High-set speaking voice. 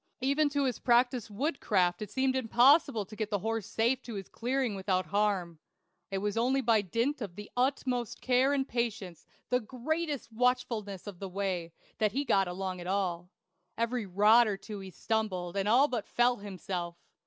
Yes: high, 220 Hz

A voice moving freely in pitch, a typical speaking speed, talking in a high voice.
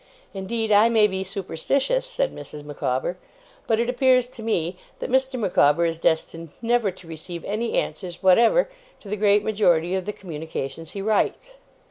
Yes: wide, 5.7 semitones; average, 165 wpm; high, 200 Hz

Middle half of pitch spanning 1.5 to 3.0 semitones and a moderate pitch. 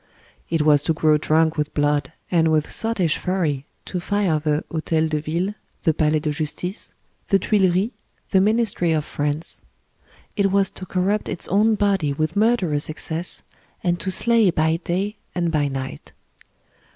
No: average, 4.1 semitones; medium, 165 Hz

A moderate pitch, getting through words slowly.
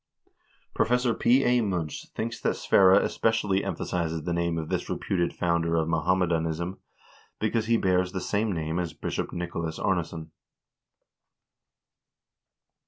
No: very low, 90 Hz; slow, 130 wpm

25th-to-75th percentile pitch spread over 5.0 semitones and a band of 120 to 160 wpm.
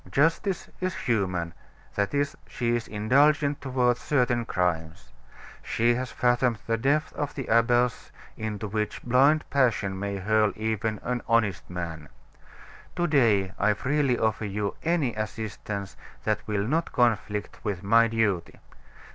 No: average, 4.0 semitones; average, 140 wpm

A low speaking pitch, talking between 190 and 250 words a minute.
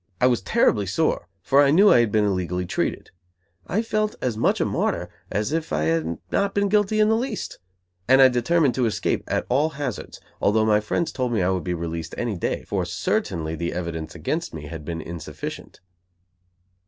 Yes: low, 110 Hz; average, 200 wpm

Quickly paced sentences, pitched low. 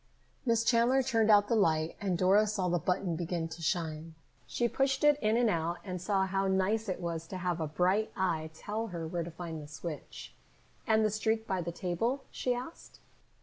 No: fast, 215 wpm; high, 190 Hz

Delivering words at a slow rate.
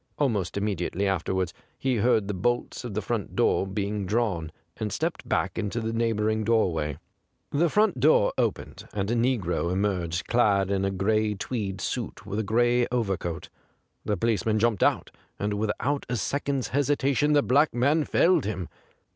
No: average, 165 wpm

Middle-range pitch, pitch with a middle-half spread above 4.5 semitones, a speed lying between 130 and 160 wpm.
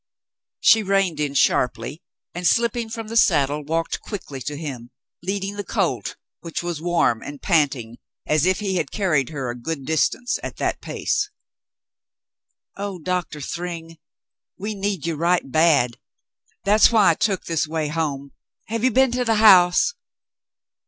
Yes: medium, 170 Hz; wide, 5.5 semitones; average, 155 wpm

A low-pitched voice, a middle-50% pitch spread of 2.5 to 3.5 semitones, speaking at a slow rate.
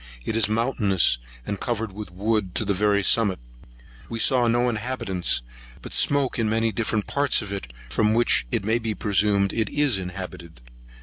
No: low, 105 Hz; average, 2.9 semitones; average, 175 wpm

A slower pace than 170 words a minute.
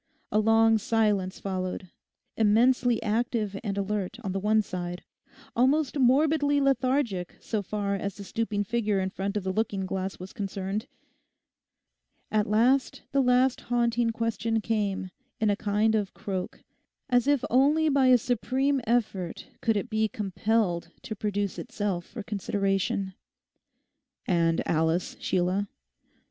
Yes: slow, 135 wpm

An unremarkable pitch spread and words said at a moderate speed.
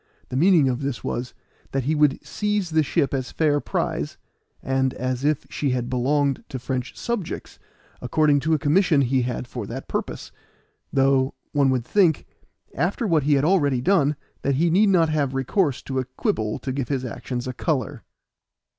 Yes: average, 3.4 semitones; average, 180 wpm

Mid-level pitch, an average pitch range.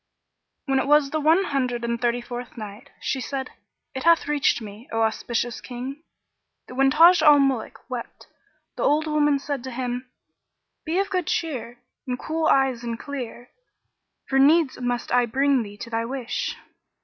No: very high, 265 Hz; average, 3.5 semitones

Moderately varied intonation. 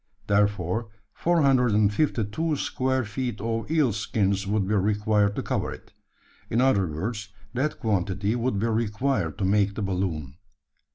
Yes: average, 3.6 semitones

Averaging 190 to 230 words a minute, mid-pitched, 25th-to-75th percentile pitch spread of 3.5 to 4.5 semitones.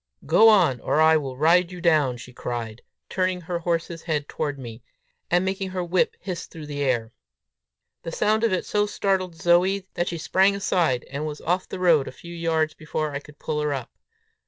Yes: fast, 205 wpm; medium, 165 Hz; average, 3.8 semitones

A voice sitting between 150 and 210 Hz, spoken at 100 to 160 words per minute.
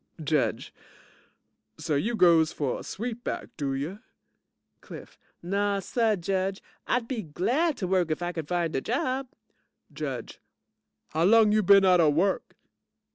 Yes: high, 190 Hz; average, 145 wpm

